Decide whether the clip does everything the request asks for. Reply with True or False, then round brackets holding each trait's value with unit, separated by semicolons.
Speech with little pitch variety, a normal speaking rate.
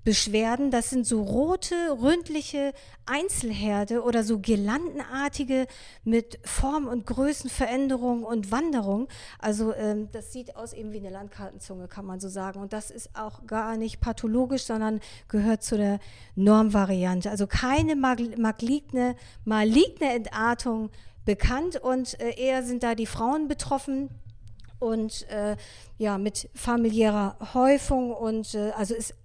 False (3.5 semitones; 135 wpm)